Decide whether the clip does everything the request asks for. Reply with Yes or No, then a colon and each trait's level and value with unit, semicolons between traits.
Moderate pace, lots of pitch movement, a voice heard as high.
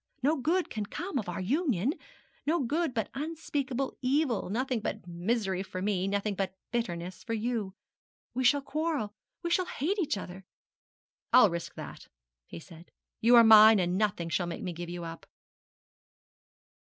Yes: average, 165 wpm; wide, 6.7 semitones; high, 220 Hz